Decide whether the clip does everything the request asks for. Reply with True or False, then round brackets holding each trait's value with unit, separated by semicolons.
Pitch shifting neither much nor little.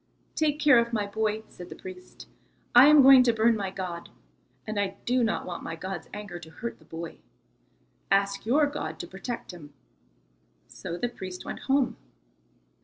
True (5.0 semitones)